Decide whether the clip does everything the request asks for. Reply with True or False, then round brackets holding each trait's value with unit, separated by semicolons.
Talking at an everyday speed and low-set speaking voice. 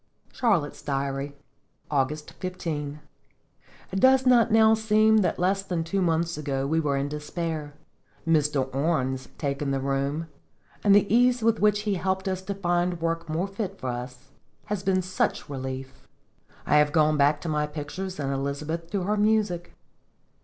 False (160 wpm; 165 Hz)